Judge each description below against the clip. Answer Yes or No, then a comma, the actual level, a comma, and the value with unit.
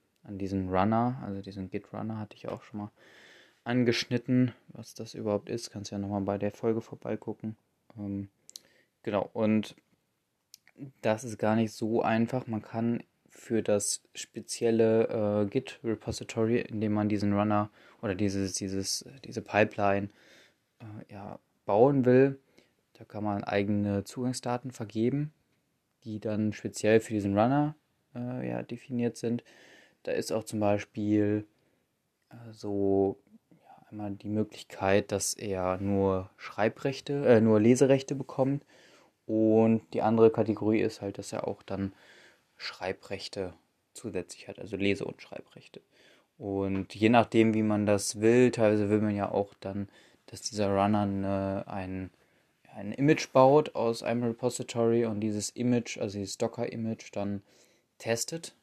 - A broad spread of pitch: No, narrow, 2.6 semitones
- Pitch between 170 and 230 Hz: No, low, 110 Hz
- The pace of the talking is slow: No, average, 140 wpm